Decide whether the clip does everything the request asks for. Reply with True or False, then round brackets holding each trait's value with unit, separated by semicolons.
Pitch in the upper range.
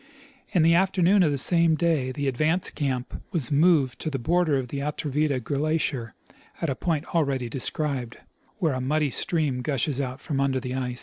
False (145 Hz)